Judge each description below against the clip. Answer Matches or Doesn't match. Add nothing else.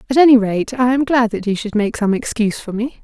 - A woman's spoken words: Matches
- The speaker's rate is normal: Doesn't match